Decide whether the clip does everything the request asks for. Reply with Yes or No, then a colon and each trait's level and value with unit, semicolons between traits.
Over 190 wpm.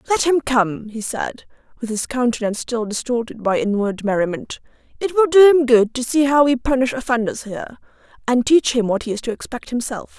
Yes: average, 200 wpm